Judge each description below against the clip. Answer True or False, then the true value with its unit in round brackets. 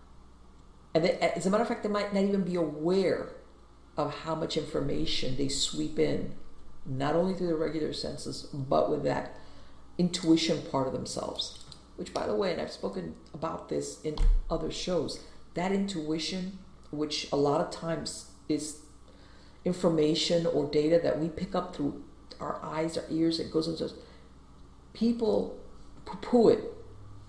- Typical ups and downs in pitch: False (8.0 semitones)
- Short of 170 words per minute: True (155 wpm)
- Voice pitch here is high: False (155 Hz)